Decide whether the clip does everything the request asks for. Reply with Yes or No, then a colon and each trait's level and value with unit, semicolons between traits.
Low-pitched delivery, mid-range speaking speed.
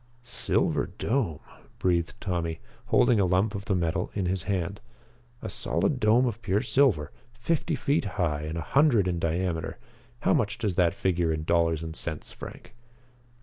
Yes: very low, 95 Hz; average, 165 wpm